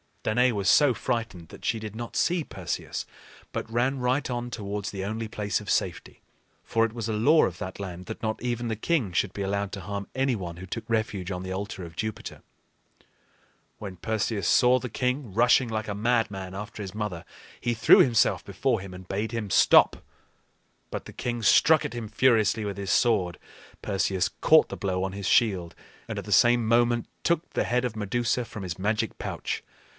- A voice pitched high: No, low, 110 Hz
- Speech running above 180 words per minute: Yes, average, 200 wpm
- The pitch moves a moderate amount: Yes, average, 3.4 semitones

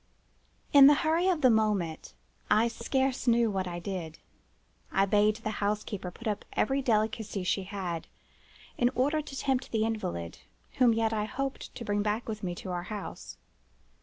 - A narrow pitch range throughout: No, average, 4.0 semitones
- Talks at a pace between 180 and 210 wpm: No, average, 170 wpm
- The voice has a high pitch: Yes, high, 215 Hz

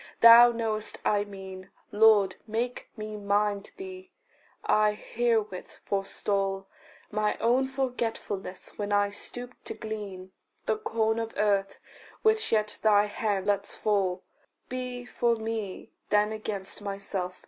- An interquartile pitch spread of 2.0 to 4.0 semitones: Yes, narrow, 2.4 semitones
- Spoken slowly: Yes, slow, 125 wpm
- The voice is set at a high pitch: Yes, high, 210 Hz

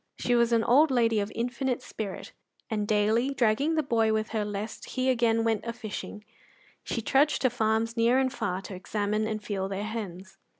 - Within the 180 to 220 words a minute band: Yes, average, 195 wpm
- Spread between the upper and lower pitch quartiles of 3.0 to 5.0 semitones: No, narrow, 2.5 semitones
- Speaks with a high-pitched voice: Yes, high, 225 Hz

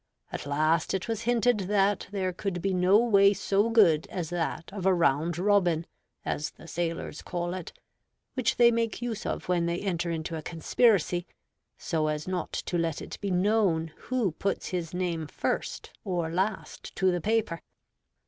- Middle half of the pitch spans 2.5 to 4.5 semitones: Yes, average, 3.5 semitones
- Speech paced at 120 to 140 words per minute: No, average, 175 wpm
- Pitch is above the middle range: No, medium, 180 Hz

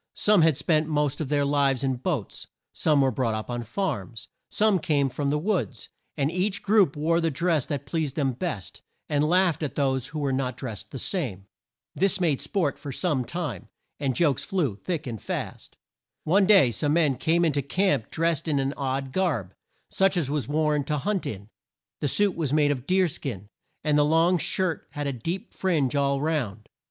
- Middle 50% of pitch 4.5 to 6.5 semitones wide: No, average, 4.1 semitones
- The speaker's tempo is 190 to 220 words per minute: Yes, average, 200 wpm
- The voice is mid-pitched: Yes, medium, 150 Hz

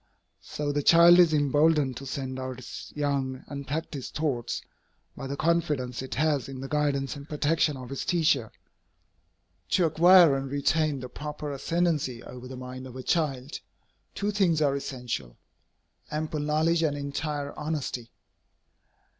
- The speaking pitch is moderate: Yes, medium, 145 Hz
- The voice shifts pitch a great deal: No, average, 3.0 semitones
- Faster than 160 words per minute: No, average, 145 wpm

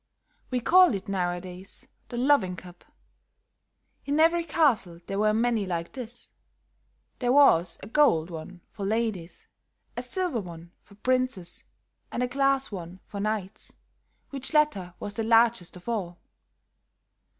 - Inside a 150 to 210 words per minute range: No, average, 140 wpm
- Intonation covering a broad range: Yes, wide, 6.0 semitones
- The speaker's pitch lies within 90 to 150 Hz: No, high, 215 Hz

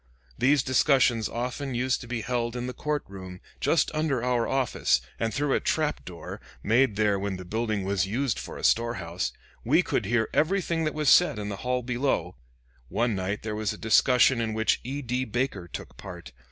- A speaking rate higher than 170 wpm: Yes, average, 200 wpm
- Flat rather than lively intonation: No, average, 4.3 semitones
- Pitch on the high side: No, low, 120 Hz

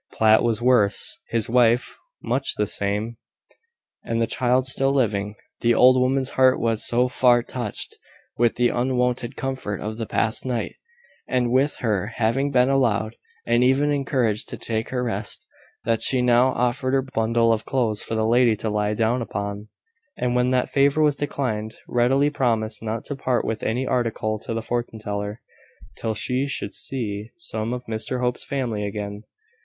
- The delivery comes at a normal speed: Yes, average, 170 wpm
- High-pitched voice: No, low, 120 Hz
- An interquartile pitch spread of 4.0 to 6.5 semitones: No, average, 2.7 semitones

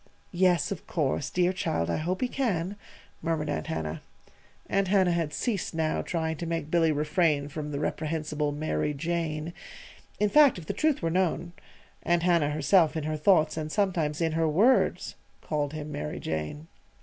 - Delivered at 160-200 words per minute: Yes, average, 175 wpm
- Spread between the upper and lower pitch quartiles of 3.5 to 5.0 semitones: No, average, 2.9 semitones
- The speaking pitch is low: No, medium, 160 Hz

